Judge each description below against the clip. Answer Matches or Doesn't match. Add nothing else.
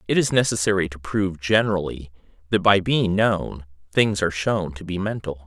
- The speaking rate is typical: Matches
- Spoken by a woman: Doesn't match